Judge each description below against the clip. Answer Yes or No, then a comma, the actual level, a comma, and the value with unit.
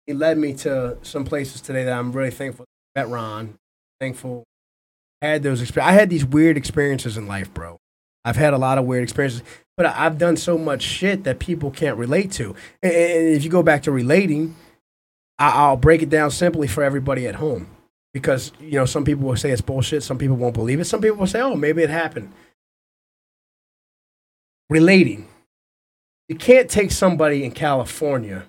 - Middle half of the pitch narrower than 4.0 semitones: No, average, 4.5 semitones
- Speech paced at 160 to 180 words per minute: No, average, 190 wpm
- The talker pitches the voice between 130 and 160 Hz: Yes, medium, 140 Hz